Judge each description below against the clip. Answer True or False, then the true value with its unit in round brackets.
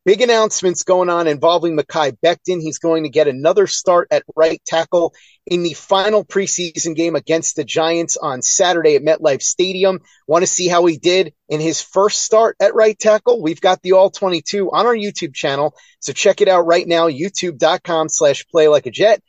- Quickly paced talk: False (195 wpm)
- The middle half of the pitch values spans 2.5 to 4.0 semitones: True (3.3 semitones)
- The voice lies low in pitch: False (175 Hz)